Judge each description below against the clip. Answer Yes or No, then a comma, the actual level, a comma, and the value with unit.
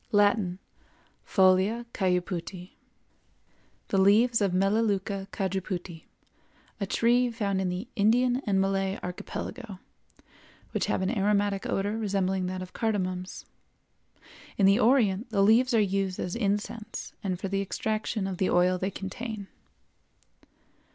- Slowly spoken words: Yes, slow, 125 wpm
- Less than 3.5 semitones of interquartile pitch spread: Yes, narrow, 2.6 semitones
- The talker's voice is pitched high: Yes, high, 195 Hz